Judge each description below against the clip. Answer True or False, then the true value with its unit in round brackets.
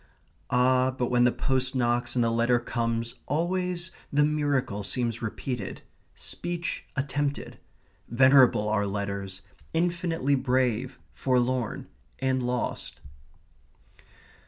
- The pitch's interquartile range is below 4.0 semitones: True (3.1 semitones)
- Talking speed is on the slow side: True (105 wpm)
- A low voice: True (125 Hz)